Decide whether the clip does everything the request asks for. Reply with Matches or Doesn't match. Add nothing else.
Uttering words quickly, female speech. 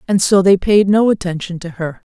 Matches